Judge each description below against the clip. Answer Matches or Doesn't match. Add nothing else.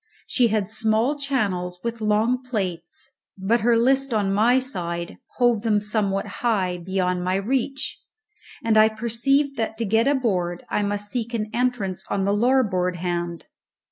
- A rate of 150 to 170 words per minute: Matches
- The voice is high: Matches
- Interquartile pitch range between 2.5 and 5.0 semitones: Matches